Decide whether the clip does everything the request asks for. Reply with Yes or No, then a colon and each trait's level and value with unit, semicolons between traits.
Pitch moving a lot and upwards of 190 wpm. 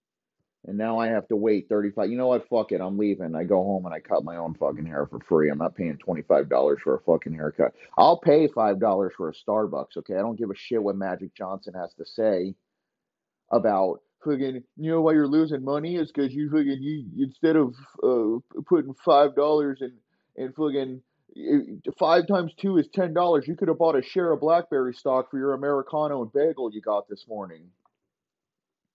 Yes: wide, 7.0 semitones; average, 200 wpm